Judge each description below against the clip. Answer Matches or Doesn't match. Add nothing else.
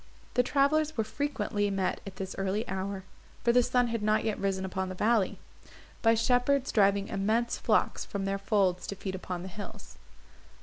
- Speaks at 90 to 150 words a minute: Doesn't match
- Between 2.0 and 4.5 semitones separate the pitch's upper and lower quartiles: Matches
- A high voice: Matches